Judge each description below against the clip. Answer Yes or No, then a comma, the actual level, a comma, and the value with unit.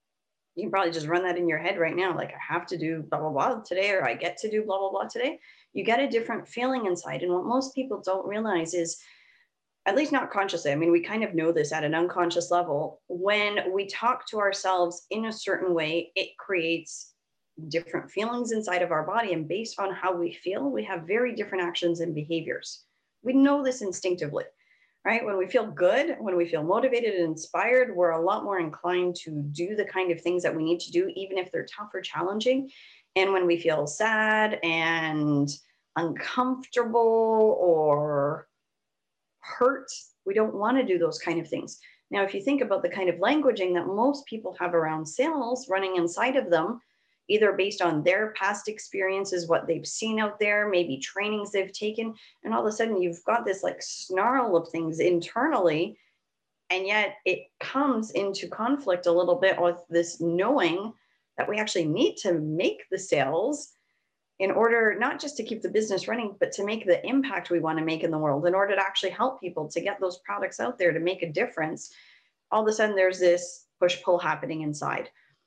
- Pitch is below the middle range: No, high, 190 Hz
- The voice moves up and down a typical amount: Yes, average, 4.4 semitones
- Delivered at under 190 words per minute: No, fast, 205 wpm